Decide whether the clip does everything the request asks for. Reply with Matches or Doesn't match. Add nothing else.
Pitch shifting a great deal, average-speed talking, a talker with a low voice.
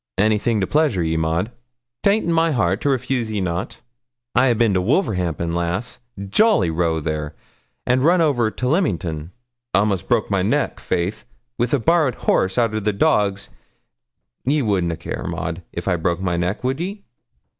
Matches